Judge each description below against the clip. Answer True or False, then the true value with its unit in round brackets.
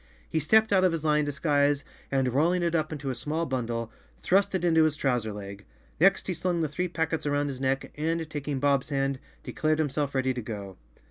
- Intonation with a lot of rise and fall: False (3.5 semitones)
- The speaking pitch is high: False (145 Hz)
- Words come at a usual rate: False (215 wpm)